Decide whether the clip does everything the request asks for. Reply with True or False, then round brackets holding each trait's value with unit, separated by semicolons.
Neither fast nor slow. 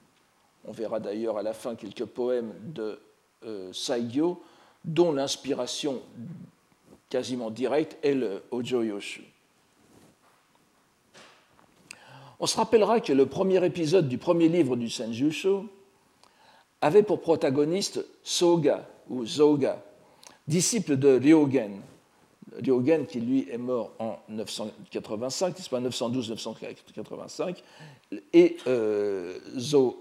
False (100 wpm)